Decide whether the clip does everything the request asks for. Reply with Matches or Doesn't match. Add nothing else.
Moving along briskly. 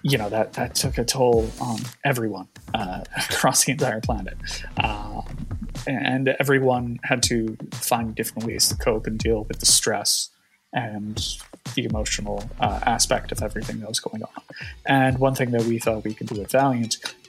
Doesn't match